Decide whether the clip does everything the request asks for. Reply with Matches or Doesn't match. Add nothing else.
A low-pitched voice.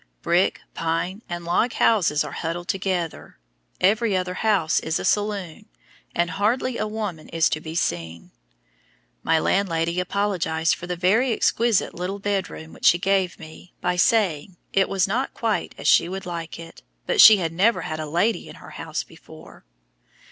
Doesn't match